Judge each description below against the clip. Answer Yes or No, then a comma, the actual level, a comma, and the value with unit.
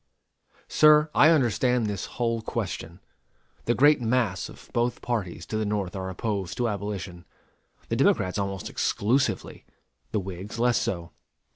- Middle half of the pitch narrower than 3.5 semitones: No, average, 4.2 semitones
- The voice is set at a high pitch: No, low, 105 Hz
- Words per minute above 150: No, average, 140 wpm